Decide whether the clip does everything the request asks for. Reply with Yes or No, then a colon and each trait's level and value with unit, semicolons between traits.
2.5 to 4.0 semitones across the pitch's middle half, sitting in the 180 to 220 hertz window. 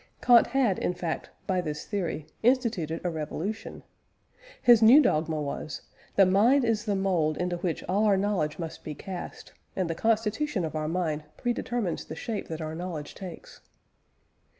No: wide, 5.4 semitones; medium, 185 Hz